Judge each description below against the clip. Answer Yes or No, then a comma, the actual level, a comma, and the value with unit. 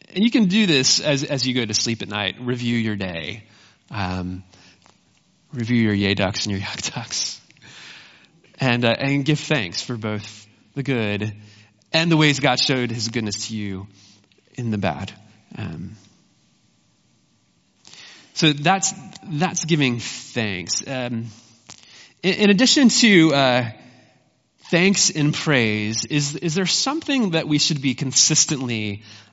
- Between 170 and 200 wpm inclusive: No, average, 145 wpm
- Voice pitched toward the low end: Yes, low, 125 Hz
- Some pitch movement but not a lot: No, wide, 6.5 semitones